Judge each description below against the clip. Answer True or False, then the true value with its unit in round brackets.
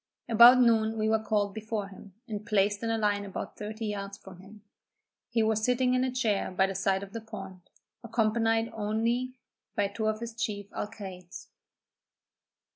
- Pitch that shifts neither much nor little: False (2.1 semitones)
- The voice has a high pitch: True (215 Hz)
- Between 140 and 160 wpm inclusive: False (175 wpm)